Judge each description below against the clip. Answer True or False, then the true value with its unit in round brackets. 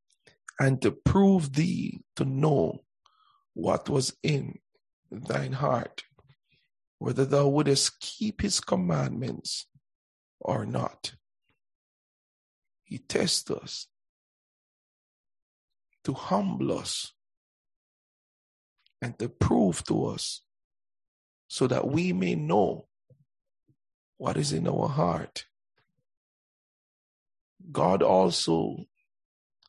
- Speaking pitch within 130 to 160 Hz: True (140 Hz)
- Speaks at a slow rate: True (85 wpm)